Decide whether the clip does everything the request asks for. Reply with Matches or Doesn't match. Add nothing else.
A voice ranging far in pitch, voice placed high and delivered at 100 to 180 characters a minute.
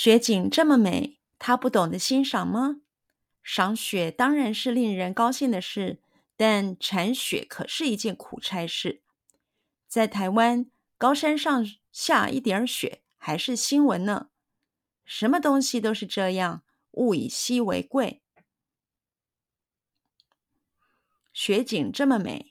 Doesn't match